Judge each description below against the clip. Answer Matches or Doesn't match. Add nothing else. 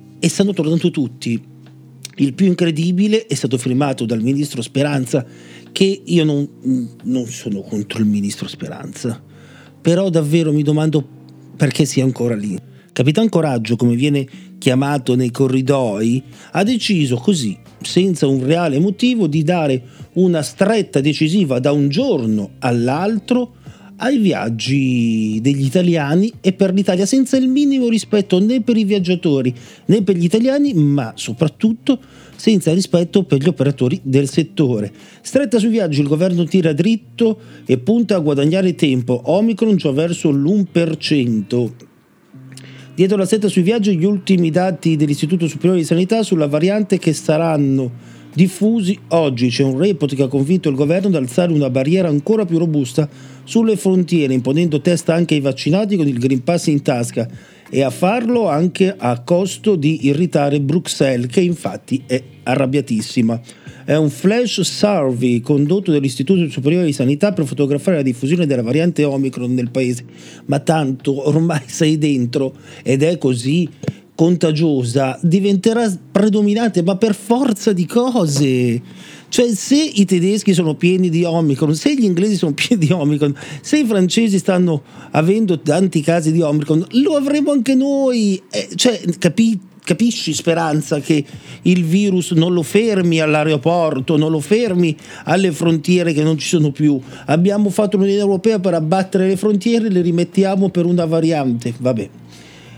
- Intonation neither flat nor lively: Doesn't match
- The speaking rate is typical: Matches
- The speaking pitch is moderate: Matches